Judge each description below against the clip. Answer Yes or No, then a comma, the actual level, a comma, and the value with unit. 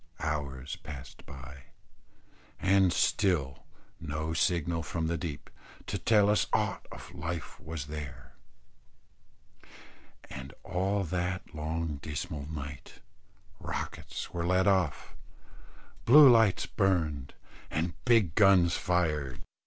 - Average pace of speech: No, slow, 105 wpm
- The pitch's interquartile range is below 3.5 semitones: No, average, 4.1 semitones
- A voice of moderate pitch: No, very low, 80 Hz